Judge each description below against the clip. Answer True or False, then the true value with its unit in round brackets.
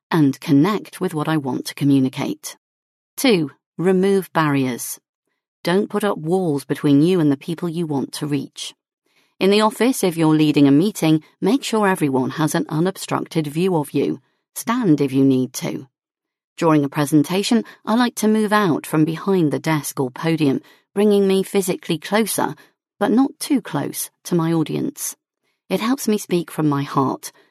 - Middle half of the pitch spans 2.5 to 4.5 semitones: False (5.1 semitones)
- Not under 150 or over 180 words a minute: True (170 wpm)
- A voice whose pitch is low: False (165 Hz)